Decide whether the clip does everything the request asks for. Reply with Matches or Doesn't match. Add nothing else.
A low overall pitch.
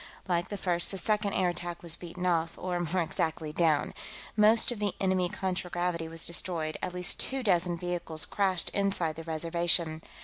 Doesn't match